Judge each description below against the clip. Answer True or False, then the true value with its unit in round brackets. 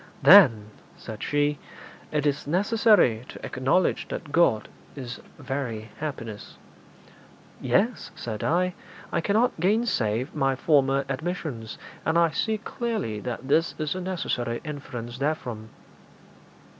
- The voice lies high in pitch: False (145 Hz)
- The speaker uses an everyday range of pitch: False (6.5 semitones)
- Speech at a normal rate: False (120 wpm)